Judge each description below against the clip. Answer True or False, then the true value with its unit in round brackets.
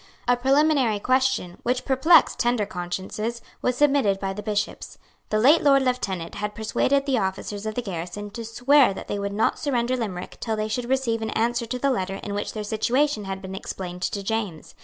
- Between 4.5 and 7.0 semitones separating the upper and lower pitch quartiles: False (4.1 semitones)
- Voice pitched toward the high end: True (220 Hz)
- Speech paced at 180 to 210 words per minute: True (200 wpm)